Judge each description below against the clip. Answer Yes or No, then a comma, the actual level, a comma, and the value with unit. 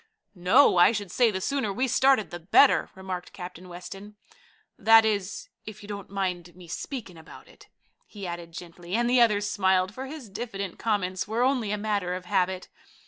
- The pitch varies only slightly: No, average, 3.5 semitones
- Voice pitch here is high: Yes, high, 200 Hz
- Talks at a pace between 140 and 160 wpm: No, average, 185 wpm